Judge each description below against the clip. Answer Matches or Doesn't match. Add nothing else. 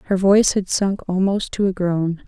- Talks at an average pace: Doesn't match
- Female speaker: Matches